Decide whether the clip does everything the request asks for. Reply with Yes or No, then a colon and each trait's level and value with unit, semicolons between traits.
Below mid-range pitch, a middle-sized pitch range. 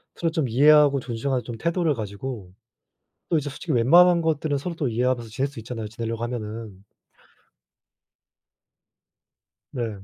Yes: low, 125 Hz; average, 4.8 semitones